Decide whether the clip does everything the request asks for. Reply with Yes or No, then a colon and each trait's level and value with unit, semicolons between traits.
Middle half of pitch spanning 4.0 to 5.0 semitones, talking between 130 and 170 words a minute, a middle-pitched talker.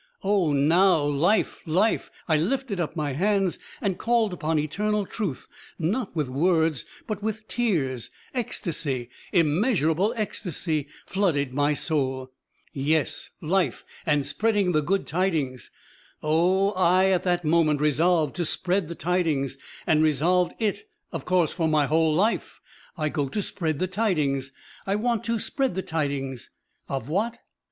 Yes: average, 4.6 semitones; average, 145 wpm; medium, 170 Hz